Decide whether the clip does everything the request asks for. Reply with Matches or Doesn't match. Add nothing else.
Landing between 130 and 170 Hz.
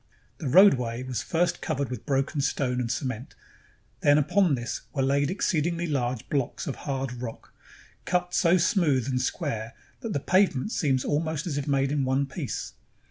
Matches